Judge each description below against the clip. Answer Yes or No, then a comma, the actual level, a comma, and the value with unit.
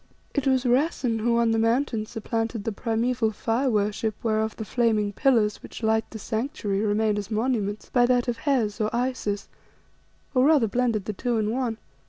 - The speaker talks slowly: No, average, 180 wpm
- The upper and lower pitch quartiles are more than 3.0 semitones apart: No, narrow, 2.6 semitones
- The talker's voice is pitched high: Yes, high, 225 Hz